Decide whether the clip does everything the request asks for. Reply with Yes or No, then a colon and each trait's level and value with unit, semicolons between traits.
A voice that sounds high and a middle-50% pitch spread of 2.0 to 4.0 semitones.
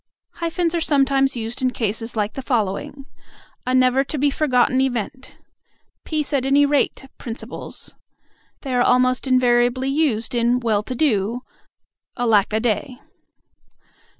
Yes: very high, 255 Hz; average, 2.8 semitones